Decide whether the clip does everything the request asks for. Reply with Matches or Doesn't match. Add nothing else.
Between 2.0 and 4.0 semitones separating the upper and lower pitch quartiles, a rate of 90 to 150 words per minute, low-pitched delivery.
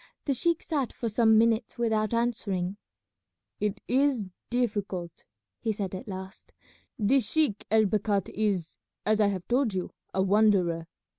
Doesn't match